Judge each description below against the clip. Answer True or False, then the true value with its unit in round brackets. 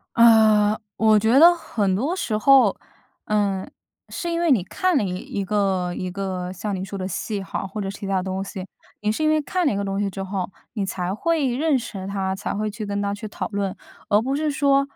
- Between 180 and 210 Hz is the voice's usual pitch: True (205 Hz)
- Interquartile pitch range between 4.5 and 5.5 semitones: True (4.8 semitones)